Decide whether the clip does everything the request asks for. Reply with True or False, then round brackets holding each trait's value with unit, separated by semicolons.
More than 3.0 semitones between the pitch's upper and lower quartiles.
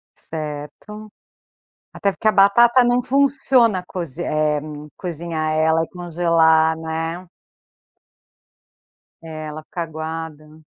True (4.1 semitones)